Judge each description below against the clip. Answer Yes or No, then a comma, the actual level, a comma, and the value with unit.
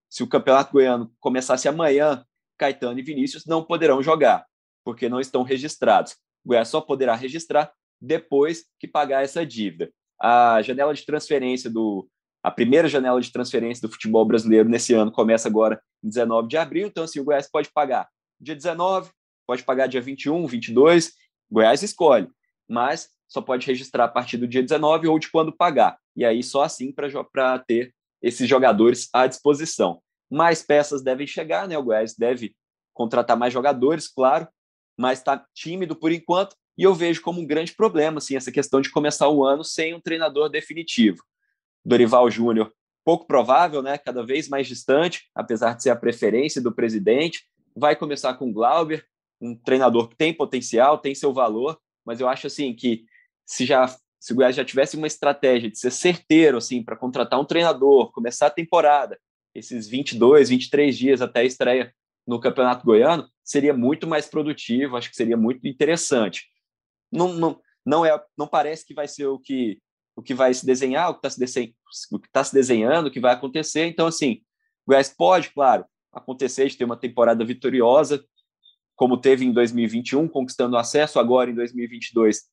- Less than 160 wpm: No, average, 175 wpm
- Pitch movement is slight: No, average, 4.2 semitones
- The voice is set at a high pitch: No, low, 135 Hz